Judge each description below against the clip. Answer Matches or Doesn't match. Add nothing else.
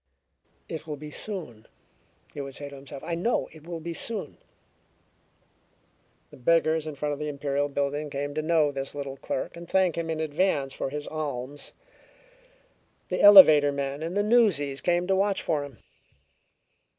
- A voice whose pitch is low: Doesn't match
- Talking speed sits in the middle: Matches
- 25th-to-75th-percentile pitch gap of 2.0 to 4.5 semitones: Matches